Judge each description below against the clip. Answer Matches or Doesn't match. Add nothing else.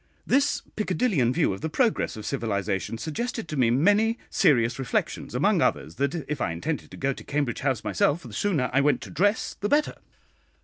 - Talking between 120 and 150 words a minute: Doesn't match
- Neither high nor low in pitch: Matches